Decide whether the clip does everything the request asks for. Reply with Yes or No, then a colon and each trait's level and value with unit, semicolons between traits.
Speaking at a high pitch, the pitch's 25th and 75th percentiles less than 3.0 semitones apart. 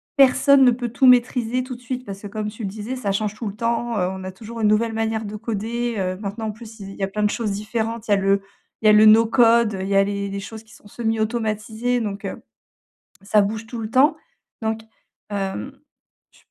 Yes: high, 220 Hz; narrow, 2.4 semitones